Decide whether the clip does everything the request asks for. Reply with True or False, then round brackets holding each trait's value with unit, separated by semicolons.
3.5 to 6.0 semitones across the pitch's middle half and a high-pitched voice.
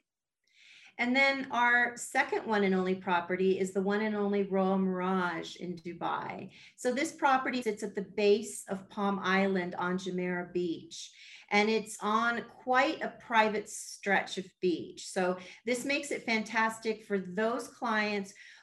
True (4.1 semitones; 210 Hz)